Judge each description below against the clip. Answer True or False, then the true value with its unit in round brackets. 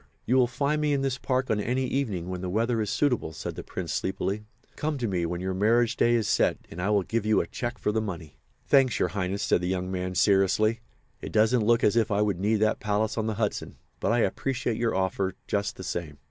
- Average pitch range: True (4.0 semitones)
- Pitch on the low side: True (105 Hz)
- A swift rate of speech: True (245 wpm)